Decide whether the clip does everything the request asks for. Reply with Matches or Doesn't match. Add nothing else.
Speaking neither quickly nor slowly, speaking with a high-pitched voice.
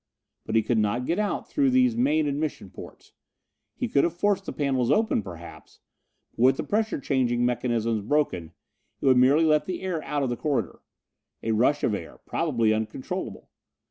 Doesn't match